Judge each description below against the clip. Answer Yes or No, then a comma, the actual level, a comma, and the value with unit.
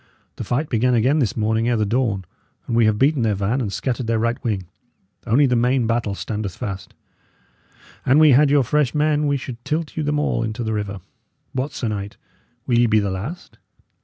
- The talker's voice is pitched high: No, low, 120 Hz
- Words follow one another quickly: Yes, fast, 210 wpm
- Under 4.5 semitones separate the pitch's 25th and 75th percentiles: Yes, average, 4.1 semitones